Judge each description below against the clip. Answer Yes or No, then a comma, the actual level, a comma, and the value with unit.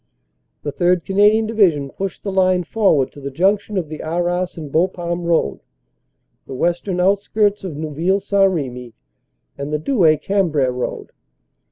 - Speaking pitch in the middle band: Yes, medium, 175 Hz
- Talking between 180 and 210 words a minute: No, average, 150 wpm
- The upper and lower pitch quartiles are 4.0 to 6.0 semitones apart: Yes, average, 4.4 semitones